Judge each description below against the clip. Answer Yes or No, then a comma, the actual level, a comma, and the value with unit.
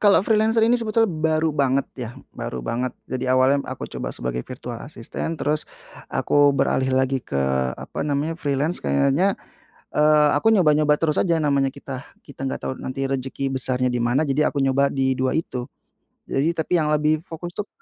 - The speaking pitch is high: No, medium, 140 Hz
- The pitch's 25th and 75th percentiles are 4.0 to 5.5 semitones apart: No, average, 3.2 semitones